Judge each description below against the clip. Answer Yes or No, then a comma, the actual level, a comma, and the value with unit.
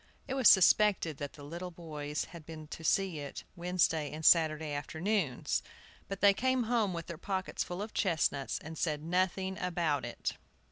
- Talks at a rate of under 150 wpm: No, average, 175 wpm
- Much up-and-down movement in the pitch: No, average, 3.7 semitones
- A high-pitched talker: No, medium, 170 Hz